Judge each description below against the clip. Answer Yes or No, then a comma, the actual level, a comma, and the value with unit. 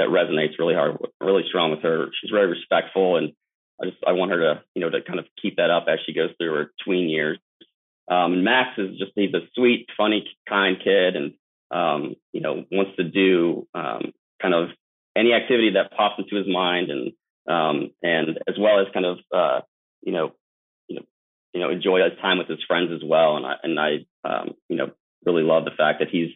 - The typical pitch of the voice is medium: No, very low, 95 Hz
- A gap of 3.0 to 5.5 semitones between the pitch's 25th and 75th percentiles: No, narrow, 2.5 semitones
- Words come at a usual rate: No, fast, 220 wpm